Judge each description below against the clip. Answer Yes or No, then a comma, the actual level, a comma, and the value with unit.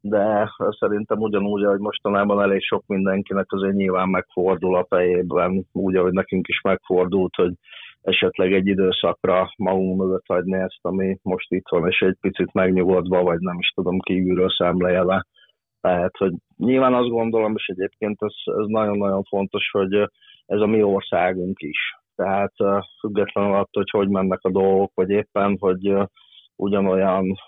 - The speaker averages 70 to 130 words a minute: No, average, 150 wpm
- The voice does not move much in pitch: Yes, narrow, 1.4 semitones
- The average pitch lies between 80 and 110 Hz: Yes, very low, 95 Hz